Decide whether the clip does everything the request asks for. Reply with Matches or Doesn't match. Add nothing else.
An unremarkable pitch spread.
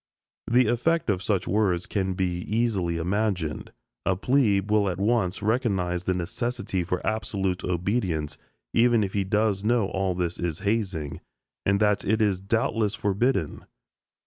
Matches